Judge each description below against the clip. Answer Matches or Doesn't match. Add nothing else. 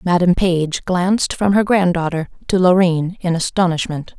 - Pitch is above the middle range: Doesn't match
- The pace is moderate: Matches